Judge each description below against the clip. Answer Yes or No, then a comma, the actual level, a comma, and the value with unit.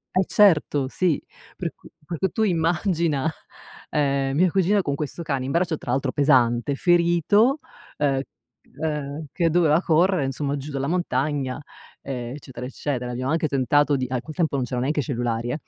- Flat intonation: No, average, 4.0 semitones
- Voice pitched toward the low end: No, medium, 145 Hz